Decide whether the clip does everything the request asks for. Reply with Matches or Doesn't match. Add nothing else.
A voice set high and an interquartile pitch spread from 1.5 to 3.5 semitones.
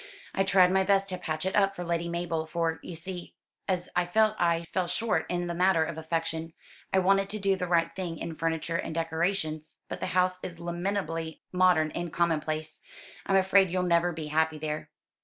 Doesn't match